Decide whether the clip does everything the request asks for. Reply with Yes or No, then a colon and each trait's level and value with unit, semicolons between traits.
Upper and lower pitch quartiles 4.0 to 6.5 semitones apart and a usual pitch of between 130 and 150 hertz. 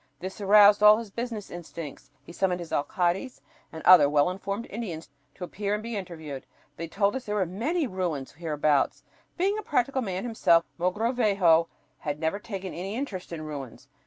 No: average, 4.5 semitones; medium, 185 Hz